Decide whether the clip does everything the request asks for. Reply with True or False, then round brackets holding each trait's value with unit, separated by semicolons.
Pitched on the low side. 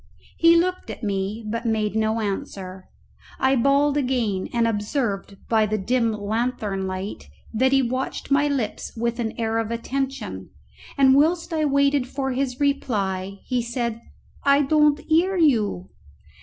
False (235 Hz)